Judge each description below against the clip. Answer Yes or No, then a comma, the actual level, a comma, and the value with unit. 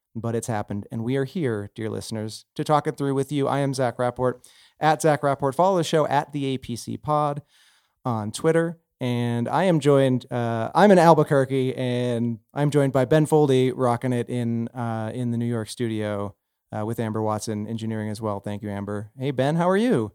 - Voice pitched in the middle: No, low, 125 Hz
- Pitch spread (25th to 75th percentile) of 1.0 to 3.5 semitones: No, average, 4.2 semitones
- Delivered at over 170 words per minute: Yes, fast, 205 wpm